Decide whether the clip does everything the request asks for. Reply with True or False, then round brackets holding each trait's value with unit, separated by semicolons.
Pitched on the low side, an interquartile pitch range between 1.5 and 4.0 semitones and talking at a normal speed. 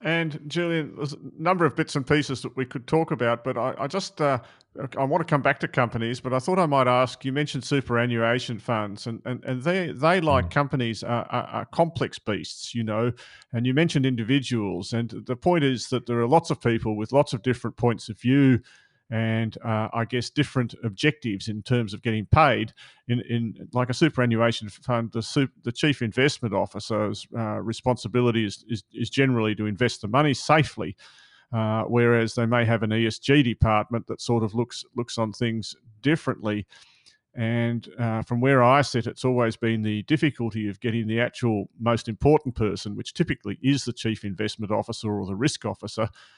True (120 Hz; 3.4 semitones; 195 wpm)